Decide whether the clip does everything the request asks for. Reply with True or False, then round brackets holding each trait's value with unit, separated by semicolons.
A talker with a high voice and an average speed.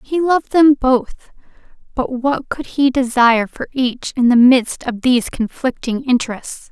True (255 Hz; 160 wpm)